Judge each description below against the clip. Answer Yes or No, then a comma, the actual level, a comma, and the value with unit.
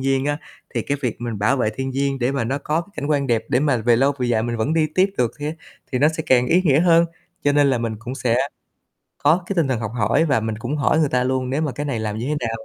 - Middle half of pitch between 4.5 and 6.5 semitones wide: No, average, 3.7 semitones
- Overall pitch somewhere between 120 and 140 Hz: Yes, low, 135 Hz